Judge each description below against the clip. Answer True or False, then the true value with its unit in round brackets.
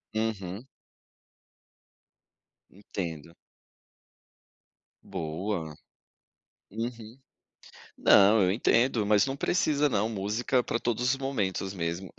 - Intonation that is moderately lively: True (4.1 semitones)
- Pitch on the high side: False (105 Hz)